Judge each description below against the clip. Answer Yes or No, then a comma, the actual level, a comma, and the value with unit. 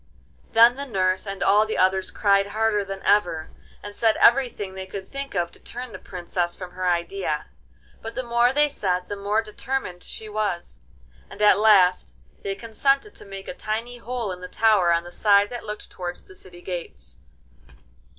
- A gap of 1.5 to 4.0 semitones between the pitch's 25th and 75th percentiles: Yes, average, 3.6 semitones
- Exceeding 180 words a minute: Yes, average, 190 wpm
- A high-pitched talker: Yes, high, 205 Hz